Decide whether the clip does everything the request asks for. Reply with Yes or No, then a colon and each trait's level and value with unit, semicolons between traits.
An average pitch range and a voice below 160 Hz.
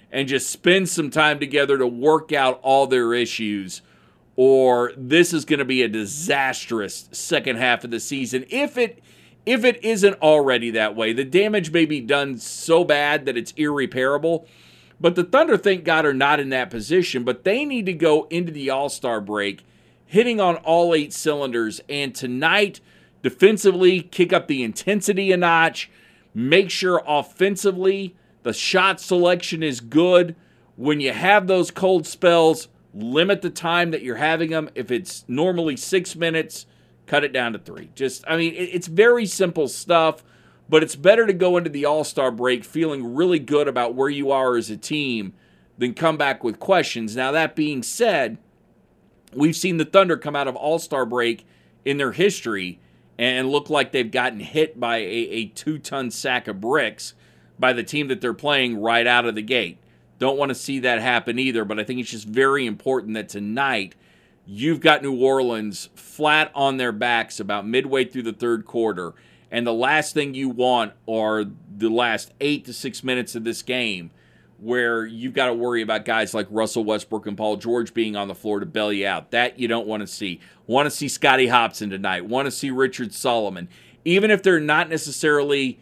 No: wide, 5.7 semitones; low, 135 Hz